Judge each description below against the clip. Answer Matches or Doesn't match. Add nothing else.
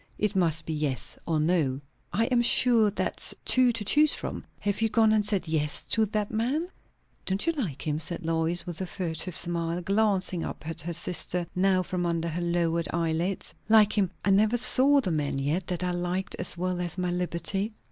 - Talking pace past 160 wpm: Matches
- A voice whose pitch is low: Doesn't match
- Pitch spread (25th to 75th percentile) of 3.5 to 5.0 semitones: Matches